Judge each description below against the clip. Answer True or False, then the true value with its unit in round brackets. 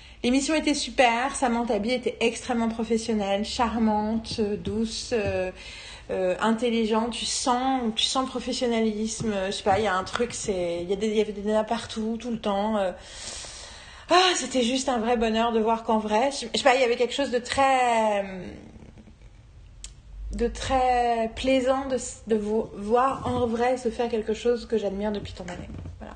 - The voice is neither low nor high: False (230 Hz)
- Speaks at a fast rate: False (180 wpm)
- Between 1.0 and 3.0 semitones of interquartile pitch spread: True (2.5 semitones)